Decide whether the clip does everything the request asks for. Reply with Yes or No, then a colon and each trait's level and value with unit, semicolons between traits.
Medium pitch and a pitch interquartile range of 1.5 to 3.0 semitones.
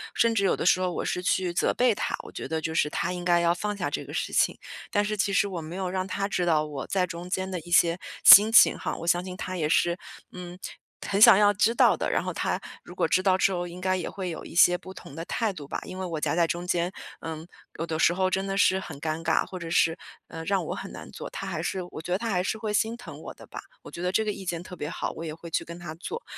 Yes: medium, 180 Hz; narrow, 2.4 semitones